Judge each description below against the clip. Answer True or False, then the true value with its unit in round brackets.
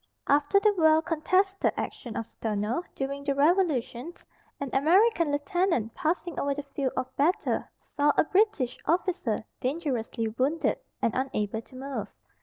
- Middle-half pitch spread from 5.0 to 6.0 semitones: True (5.3 semitones)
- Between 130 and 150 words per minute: True (140 wpm)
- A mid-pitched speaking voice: False (285 Hz)